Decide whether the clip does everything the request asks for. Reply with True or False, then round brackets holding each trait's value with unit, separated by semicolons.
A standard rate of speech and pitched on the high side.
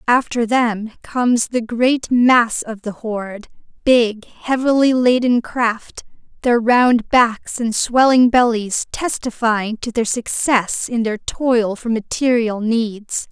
False (130 wpm; 235 Hz)